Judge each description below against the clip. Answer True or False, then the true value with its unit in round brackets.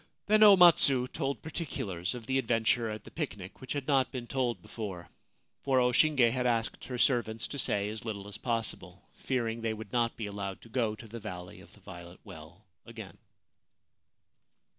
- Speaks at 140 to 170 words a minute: False (195 wpm)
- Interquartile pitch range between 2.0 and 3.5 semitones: False (4.0 semitones)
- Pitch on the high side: False (115 Hz)